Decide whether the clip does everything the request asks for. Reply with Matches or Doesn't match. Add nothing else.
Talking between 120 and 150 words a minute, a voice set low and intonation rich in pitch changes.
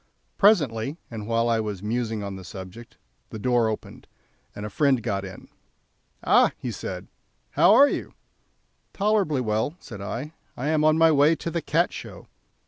Doesn't match